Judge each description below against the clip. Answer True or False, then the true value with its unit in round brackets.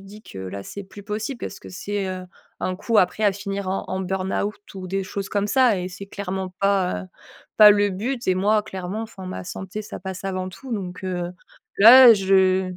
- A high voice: True (195 Hz)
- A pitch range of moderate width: False (1.9 semitones)